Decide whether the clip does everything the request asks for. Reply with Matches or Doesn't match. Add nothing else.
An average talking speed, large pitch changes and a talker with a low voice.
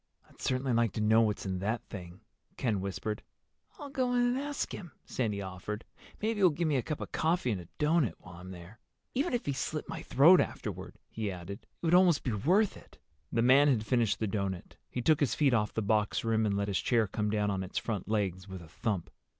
Doesn't match